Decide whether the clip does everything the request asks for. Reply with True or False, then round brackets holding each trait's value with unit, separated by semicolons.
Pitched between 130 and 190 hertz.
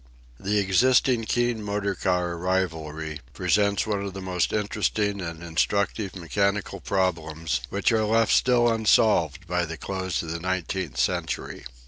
False (95 Hz)